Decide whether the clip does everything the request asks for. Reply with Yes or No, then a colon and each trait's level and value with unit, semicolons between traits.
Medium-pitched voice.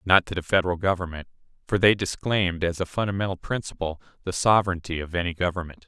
No: very low, 90 Hz